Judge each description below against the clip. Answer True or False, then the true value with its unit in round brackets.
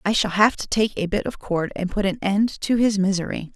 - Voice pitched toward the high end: True (200 Hz)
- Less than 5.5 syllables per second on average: True (5.3 syllables/s)